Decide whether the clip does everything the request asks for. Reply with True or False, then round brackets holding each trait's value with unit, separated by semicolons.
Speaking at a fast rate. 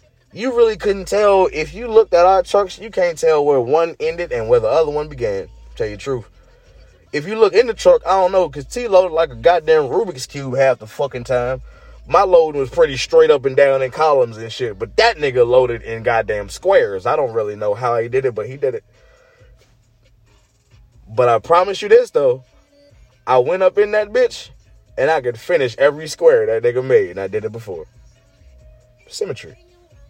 True (210 wpm)